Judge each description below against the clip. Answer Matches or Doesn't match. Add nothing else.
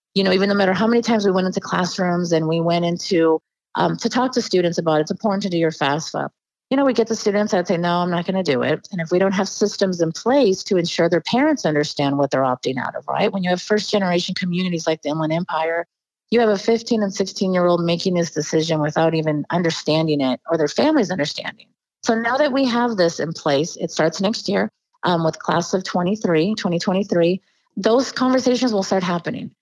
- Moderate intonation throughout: Matches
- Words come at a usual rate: Doesn't match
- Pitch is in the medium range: Matches